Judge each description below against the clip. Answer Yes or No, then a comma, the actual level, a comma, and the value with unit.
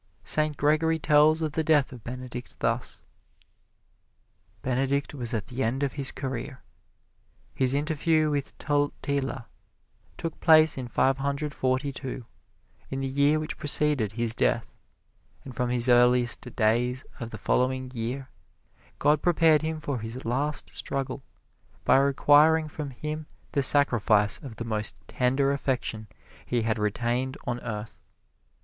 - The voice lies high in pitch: No, low, 135 Hz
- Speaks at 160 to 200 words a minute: No, average, 140 wpm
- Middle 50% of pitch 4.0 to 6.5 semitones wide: No, average, 3.3 semitones